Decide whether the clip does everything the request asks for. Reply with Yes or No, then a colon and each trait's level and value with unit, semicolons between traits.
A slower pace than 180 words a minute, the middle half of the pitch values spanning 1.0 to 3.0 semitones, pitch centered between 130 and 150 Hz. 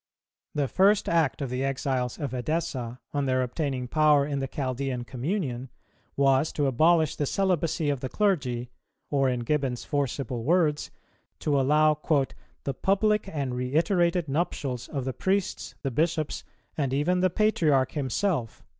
No: average, 145 wpm; average, 4.0 semitones; medium, 140 Hz